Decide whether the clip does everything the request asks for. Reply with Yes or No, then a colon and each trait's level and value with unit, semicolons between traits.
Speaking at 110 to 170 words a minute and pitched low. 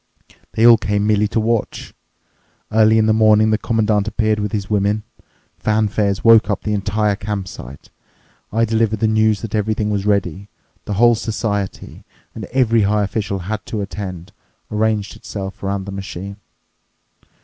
Yes: average, 150 wpm; low, 105 Hz